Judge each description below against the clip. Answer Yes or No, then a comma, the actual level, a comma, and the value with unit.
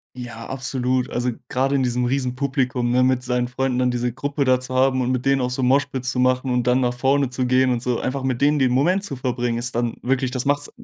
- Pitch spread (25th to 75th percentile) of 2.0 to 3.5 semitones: No, narrow, 1.3 semitones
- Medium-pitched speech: No, low, 130 Hz